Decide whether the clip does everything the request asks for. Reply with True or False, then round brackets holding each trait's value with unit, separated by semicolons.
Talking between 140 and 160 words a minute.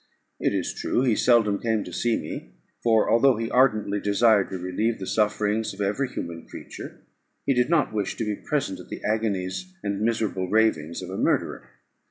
False (190 wpm)